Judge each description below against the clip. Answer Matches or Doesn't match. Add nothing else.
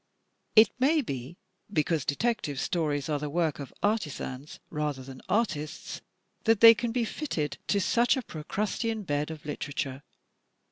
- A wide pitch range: Matches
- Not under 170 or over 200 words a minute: Doesn't match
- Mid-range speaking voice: Matches